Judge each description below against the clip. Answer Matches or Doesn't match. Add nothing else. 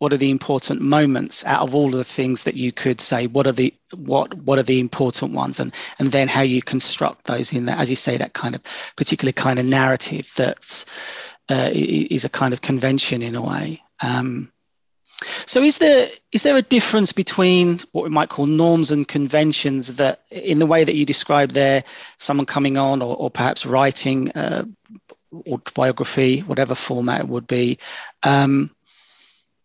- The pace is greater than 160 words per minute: Matches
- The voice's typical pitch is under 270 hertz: Matches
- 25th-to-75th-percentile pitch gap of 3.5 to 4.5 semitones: Doesn't match